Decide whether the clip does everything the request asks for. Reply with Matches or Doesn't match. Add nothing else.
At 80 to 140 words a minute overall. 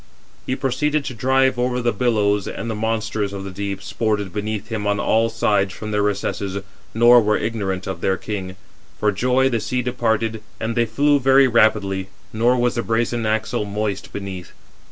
Doesn't match